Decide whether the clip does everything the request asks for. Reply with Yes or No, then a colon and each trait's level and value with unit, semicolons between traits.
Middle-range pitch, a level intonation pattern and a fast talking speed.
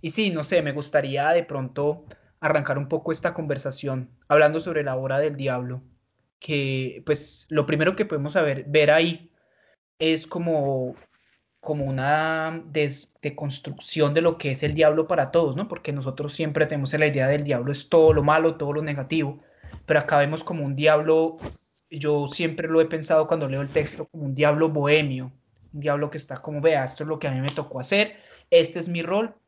Yes: medium, 150 Hz; narrow, 2.3 semitones; fast, 195 wpm